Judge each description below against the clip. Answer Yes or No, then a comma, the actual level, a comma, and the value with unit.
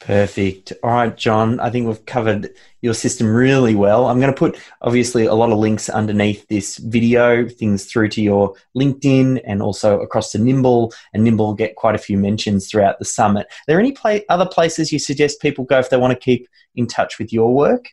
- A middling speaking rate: No, fast, 220 wpm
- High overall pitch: No, low, 115 Hz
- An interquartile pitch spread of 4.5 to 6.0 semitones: No, average, 3.3 semitones